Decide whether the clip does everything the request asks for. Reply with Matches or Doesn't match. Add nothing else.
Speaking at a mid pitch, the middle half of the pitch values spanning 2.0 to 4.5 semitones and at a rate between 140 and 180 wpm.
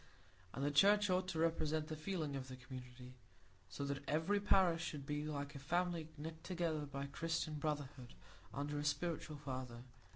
Matches